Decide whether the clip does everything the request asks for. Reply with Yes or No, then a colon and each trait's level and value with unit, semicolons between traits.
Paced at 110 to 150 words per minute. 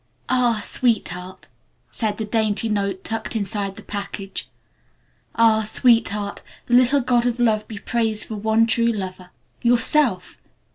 Yes: average, 140 wpm